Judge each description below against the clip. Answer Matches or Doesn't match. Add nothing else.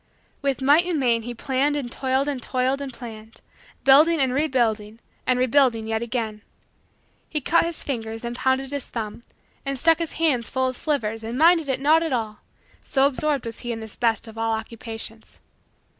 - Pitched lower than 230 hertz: Doesn't match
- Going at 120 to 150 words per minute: Doesn't match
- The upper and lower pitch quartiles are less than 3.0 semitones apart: Doesn't match